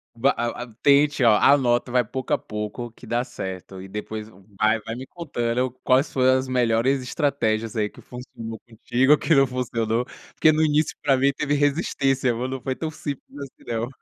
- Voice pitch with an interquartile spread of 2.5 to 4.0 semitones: Yes, average, 3.3 semitones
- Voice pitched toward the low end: Yes, low, 125 Hz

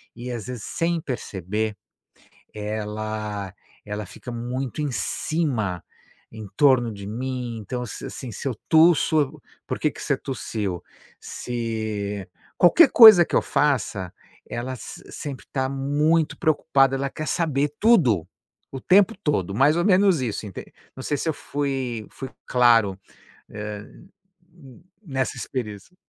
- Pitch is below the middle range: Yes, low, 125 Hz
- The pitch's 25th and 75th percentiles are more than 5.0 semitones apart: Yes, wide, 5.5 semitones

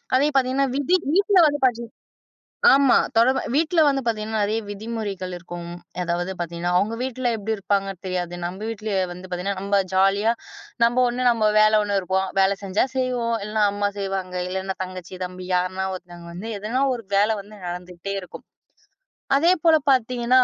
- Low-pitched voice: No, high, 205 Hz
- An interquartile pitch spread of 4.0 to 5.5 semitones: Yes, average, 4.5 semitones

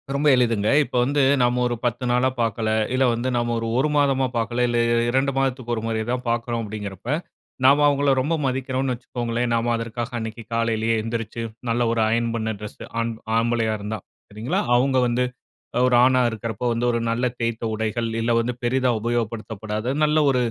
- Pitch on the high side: No, low, 120 Hz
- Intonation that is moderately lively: No, narrow, 1.9 semitones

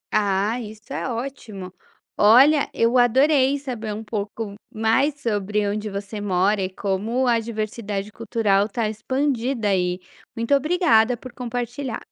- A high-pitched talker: Yes, high, 225 Hz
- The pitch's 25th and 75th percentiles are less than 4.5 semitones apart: Yes, average, 3.4 semitones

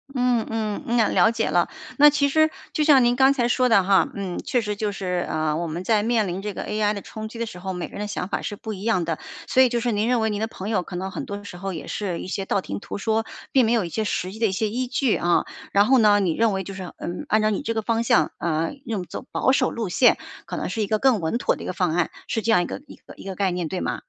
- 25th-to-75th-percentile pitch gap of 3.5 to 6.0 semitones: Yes, average, 3.8 semitones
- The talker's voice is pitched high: Yes, high, 210 Hz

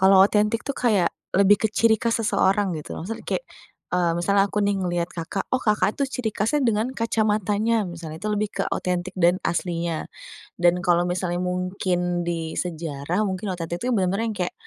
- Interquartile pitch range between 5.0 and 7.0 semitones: No, average, 3.4 semitones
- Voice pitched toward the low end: No, high, 190 Hz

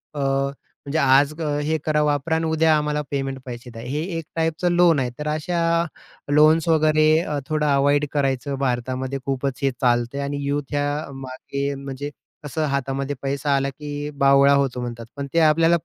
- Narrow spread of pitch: Yes, narrow, 2.1 semitones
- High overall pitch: No, medium, 140 Hz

